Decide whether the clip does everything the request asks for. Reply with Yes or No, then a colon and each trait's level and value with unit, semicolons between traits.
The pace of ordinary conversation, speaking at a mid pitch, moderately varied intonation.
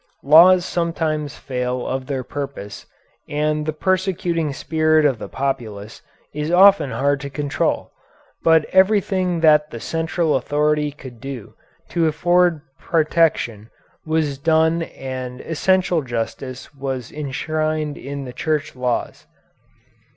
No: slow, 120 wpm; medium, 150 Hz; average, 3.5 semitones